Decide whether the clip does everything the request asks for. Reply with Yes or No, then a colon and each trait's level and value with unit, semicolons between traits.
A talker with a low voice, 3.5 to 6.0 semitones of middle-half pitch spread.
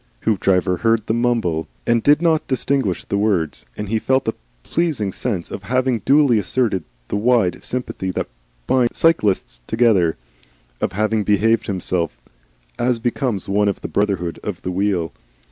Yes: low, 110 Hz; average, 4.4 semitones